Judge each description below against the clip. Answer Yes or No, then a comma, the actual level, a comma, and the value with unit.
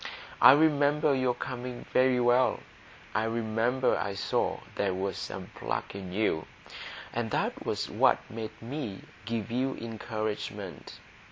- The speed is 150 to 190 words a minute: No, slow, 135 wpm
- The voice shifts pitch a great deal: No, average, 3.1 semitones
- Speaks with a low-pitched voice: Yes, low, 115 Hz